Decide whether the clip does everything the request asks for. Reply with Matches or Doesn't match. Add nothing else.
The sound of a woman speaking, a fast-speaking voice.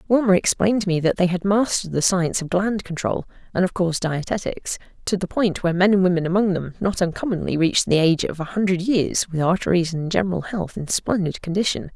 Matches